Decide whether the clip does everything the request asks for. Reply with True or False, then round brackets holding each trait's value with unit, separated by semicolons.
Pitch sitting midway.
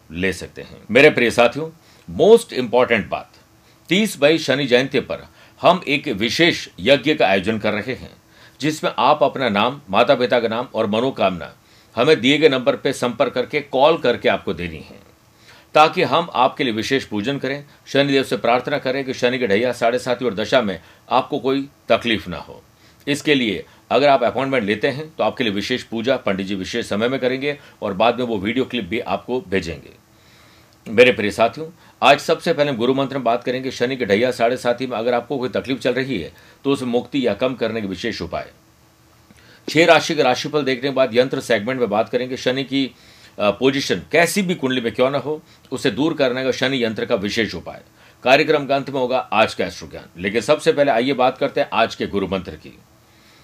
False (125 Hz)